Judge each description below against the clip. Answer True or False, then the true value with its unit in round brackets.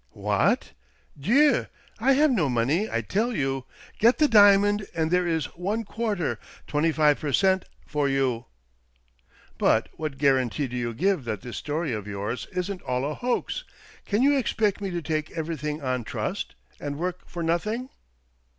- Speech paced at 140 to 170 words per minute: False (180 wpm)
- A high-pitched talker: False (160 Hz)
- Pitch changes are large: True (7.2 semitones)